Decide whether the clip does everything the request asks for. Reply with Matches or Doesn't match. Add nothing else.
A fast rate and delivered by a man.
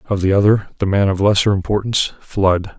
Doesn't match